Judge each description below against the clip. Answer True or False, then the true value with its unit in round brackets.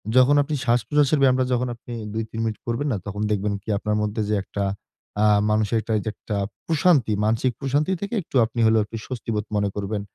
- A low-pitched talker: True (115 Hz)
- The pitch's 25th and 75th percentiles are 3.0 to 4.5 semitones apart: True (3.7 semitones)